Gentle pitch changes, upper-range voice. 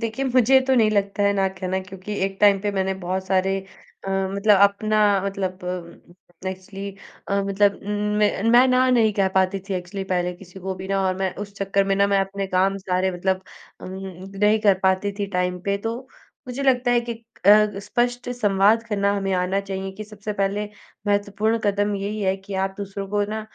Yes: narrow, 1.7 semitones; high, 200 Hz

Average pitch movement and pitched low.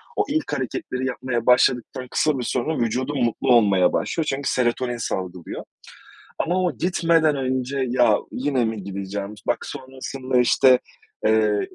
Yes: average, 3.3 semitones; low, 125 Hz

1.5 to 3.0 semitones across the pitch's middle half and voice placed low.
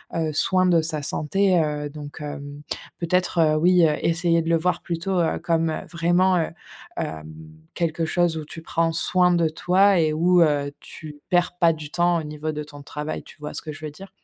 No: narrow, 2.6 semitones; medium, 165 Hz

